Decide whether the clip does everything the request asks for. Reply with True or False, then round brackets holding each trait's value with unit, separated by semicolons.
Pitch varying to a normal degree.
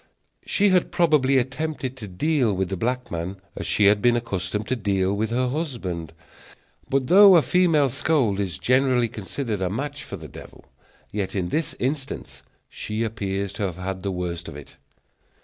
False (6.2 semitones)